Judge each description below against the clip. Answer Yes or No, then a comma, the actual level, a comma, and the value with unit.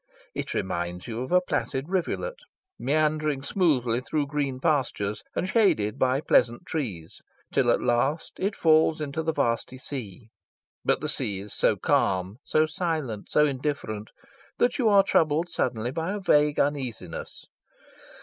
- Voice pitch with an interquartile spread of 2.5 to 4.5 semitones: No, average, 5.3 semitones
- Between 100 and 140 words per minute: No, average, 150 wpm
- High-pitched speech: No, medium, 140 Hz